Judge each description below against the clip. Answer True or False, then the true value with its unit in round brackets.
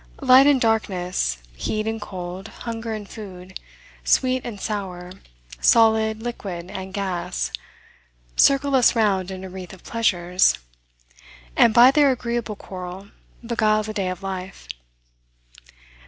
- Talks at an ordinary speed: False (125 wpm)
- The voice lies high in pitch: True (205 Hz)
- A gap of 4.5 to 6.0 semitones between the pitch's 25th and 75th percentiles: False (3.8 semitones)